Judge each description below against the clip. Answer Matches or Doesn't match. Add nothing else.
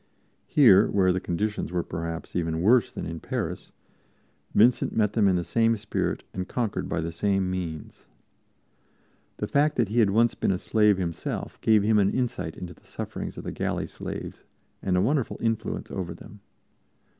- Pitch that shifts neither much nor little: Matches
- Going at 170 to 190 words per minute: Matches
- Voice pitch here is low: Matches